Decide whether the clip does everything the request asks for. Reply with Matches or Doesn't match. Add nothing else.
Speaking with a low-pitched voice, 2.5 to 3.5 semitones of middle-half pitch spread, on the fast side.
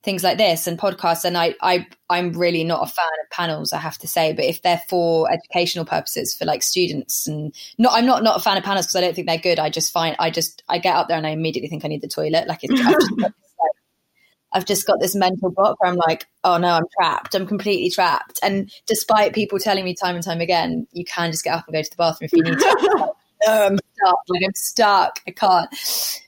Doesn't match